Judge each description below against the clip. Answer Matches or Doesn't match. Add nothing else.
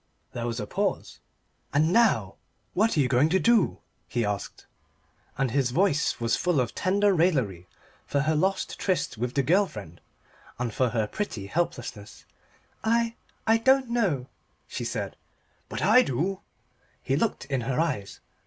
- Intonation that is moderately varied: Doesn't match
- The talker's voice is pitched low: Doesn't match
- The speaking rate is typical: Matches